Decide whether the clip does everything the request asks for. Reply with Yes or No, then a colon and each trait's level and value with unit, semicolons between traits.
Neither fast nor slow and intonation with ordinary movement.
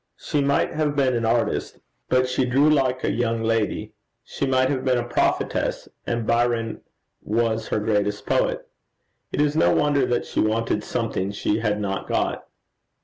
Yes: average, 170 wpm; average, 3.1 semitones